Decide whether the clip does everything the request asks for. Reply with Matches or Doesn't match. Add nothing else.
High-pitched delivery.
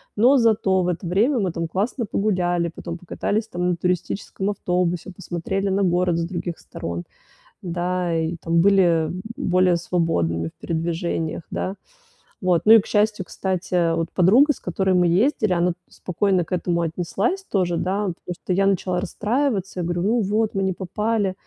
Doesn't match